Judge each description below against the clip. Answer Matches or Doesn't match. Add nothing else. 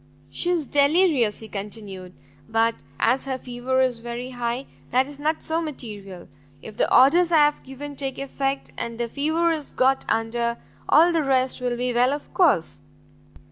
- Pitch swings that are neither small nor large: Matches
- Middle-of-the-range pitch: Doesn't match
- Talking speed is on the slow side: Doesn't match